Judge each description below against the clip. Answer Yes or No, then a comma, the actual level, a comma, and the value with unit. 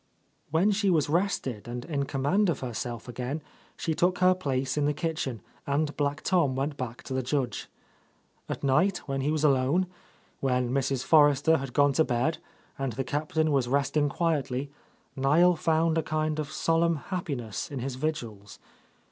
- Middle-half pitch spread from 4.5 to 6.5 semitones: No, average, 3.4 semitones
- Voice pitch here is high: No, medium, 145 Hz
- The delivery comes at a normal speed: Yes, average, 180 wpm